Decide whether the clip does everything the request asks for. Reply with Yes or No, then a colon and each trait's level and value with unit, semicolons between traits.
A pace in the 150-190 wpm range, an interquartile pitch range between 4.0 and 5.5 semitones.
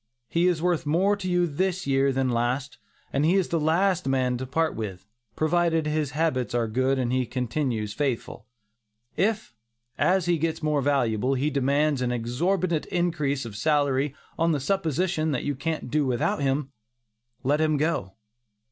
Yes: average, 170 wpm; average, 4.3 semitones